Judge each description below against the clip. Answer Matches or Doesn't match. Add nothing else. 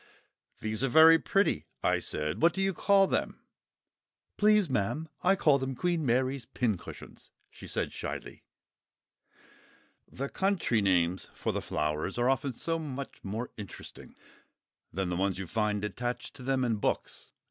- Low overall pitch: Matches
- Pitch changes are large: Matches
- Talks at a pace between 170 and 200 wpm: Doesn't match